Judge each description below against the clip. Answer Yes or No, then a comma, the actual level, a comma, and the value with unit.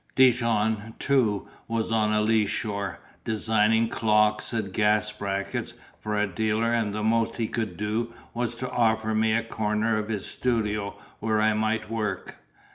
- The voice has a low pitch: Yes, low, 110 Hz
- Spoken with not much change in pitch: Yes, narrow, 1.3 semitones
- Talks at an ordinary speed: Yes, average, 155 wpm